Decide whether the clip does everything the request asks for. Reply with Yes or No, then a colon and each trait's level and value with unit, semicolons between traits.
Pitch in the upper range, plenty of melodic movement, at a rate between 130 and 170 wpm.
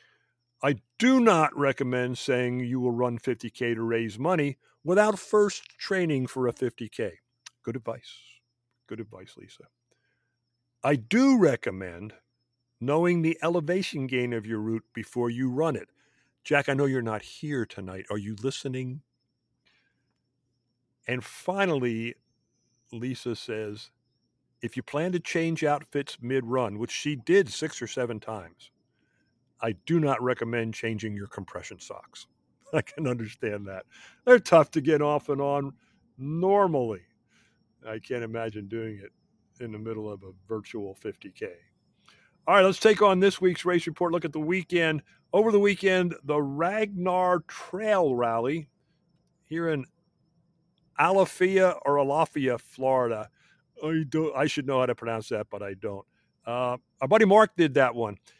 No: low, 135 Hz; wide, 6.0 semitones; average, 145 wpm